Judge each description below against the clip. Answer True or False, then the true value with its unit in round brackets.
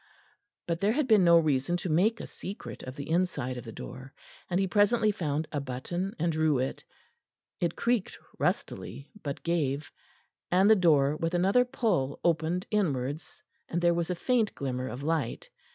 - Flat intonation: False (5.2 semitones)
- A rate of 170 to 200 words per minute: True (175 wpm)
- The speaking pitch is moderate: True (170 Hz)